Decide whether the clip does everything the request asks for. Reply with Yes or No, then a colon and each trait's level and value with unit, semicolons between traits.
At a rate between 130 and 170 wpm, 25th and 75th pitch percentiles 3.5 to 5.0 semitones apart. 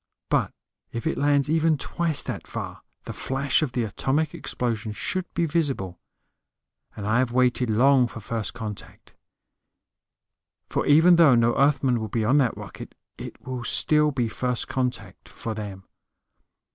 Yes: average, 155 wpm; average, 4.4 semitones